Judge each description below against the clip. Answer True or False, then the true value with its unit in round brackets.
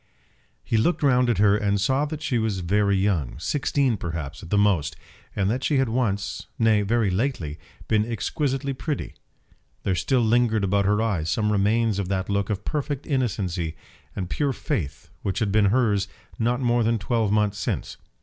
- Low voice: True (105 Hz)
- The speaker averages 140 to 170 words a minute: False (180 wpm)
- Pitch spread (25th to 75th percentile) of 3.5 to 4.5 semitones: True (3.9 semitones)